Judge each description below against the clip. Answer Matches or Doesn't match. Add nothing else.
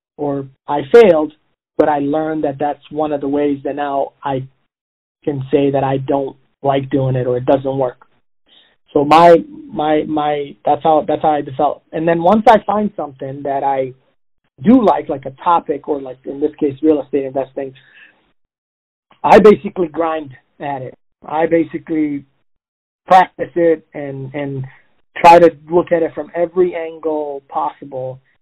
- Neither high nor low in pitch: Matches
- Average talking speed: Matches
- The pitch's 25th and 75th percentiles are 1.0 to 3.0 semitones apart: Matches